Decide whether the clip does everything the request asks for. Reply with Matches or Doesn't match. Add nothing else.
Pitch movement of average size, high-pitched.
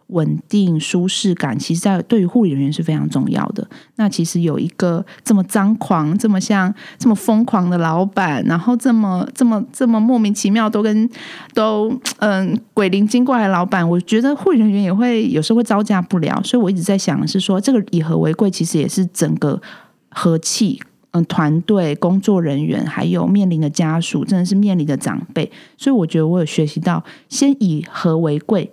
Matches